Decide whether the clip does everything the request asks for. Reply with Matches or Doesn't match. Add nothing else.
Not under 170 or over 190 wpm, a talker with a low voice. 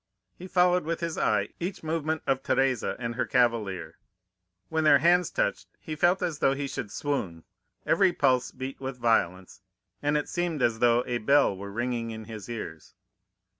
Matches